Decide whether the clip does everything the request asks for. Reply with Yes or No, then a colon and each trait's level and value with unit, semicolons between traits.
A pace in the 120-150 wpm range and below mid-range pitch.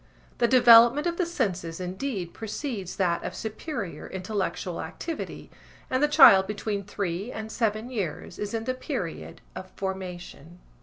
No: average, 145 wpm; high, 210 Hz